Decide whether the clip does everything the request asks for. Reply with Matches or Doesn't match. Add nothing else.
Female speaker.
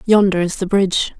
Matches